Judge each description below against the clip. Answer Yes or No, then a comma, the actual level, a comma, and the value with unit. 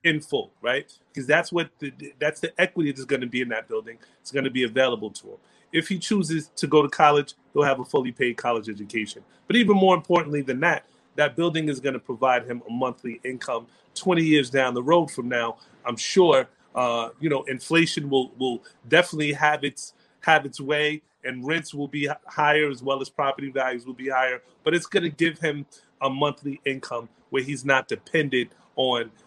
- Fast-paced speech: Yes, fast, 210 wpm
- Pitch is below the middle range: No, medium, 145 Hz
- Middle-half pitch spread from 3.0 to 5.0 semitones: Yes, average, 3.3 semitones